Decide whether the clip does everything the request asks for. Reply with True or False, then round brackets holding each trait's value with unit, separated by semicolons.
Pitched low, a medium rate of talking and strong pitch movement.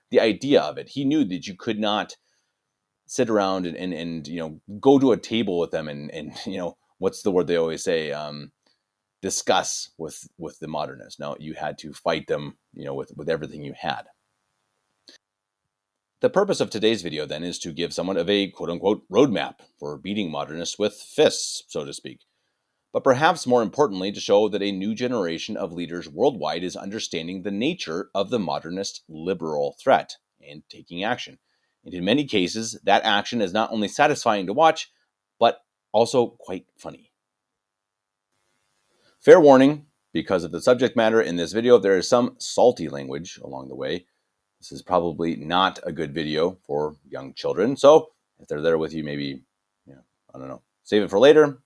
False (95 Hz; 185 wpm; 4.9 semitones)